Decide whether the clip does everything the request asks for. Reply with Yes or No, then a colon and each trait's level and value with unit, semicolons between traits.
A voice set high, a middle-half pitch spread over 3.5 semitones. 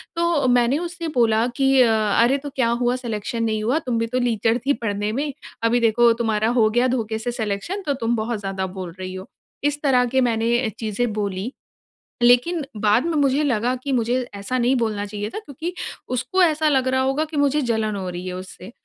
Yes: high, 240 Hz; average, 4.0 semitones